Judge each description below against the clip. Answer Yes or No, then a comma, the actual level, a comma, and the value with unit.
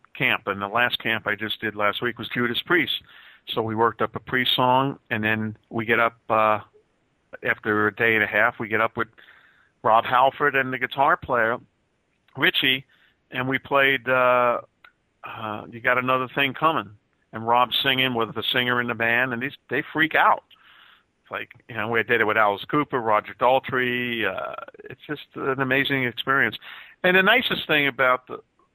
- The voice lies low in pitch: Yes, low, 120 Hz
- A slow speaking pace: No, average, 190 wpm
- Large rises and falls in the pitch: No, average, 3.0 semitones